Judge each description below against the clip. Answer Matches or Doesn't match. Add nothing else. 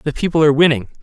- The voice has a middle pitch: Matches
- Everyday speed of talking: Doesn't match